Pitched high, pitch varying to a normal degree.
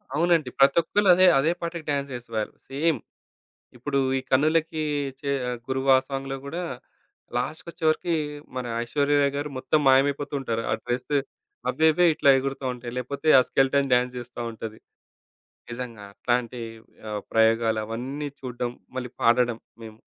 No: low, 135 Hz; average, 3.5 semitones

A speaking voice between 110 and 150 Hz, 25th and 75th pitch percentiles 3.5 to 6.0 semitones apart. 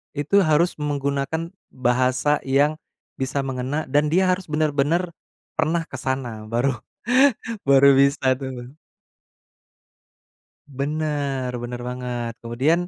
No: medium, 140 Hz; average, 2.9 semitones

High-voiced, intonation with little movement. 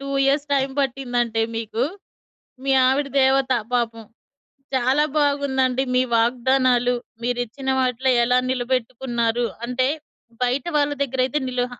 Yes: very high, 255 Hz; narrow, 1.8 semitones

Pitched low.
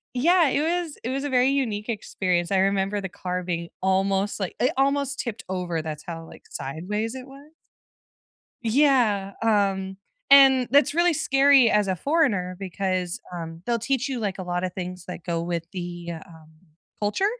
No: high, 200 Hz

